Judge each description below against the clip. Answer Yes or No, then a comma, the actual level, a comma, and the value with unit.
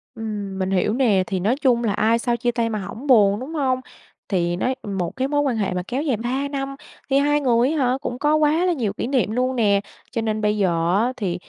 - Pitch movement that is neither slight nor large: Yes, average, 4.7 semitones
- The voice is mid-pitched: No, high, 235 Hz